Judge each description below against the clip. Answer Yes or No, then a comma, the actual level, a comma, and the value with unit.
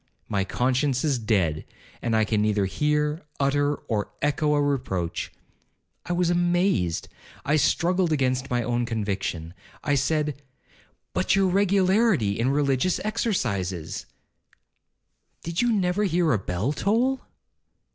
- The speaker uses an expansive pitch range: Yes, wide, 8.1 semitones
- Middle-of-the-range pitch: Yes, medium, 145 Hz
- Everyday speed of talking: No, slow, 120 wpm